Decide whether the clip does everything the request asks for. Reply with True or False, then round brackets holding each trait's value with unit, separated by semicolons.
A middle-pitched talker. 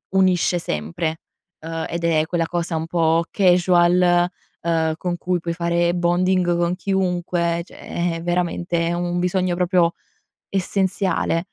True (175 Hz)